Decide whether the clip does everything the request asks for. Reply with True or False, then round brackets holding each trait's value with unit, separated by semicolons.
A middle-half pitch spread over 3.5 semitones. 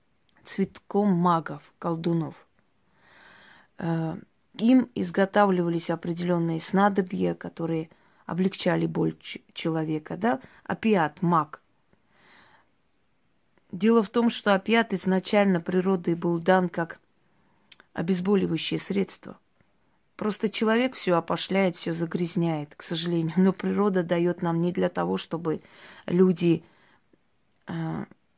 False (2.8 semitones)